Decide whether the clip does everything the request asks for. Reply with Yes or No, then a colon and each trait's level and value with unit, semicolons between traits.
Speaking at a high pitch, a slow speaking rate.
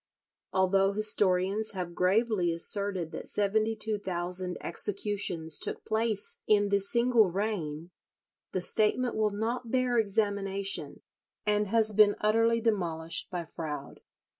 Yes: high, 205 Hz; slow, 120 wpm